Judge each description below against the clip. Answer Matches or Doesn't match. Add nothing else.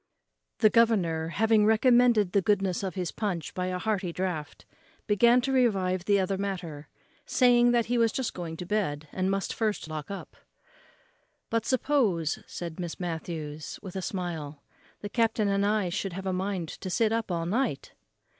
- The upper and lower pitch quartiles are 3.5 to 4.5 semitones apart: Matches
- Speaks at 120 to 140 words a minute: Doesn't match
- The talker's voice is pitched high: Matches